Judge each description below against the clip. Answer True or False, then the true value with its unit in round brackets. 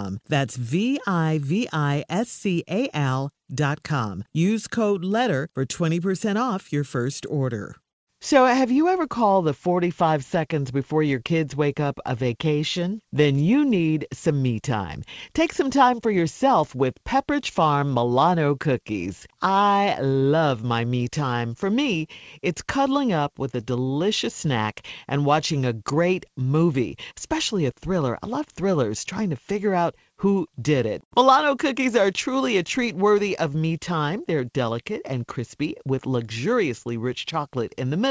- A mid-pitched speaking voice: True (155 Hz)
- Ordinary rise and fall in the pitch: False (7.1 semitones)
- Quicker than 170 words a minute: False (165 wpm)